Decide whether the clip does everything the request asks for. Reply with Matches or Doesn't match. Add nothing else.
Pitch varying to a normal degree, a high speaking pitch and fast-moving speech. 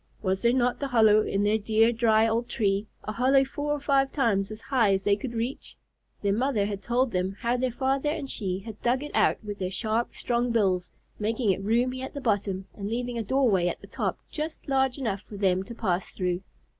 Matches